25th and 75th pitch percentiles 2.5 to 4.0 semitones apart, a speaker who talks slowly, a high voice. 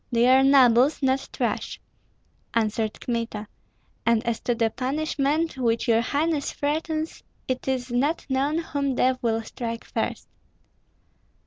Yes: average, 3.5 semitones; slow, 130 wpm; very high, 255 Hz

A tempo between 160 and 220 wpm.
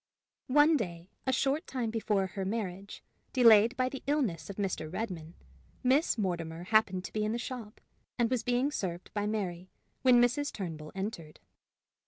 Yes: average, 165 wpm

